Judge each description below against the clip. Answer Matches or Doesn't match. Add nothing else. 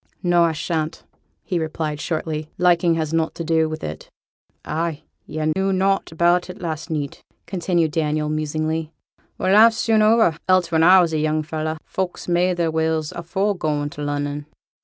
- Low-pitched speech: Doesn't match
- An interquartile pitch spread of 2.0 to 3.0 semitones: Matches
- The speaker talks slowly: Doesn't match